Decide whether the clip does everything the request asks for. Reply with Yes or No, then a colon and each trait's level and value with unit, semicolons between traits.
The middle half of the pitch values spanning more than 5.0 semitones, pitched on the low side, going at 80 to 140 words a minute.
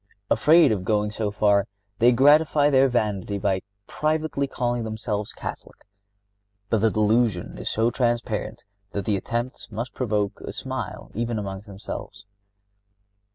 No: average, 3.1 semitones; low, 110 Hz; slow, 135 wpm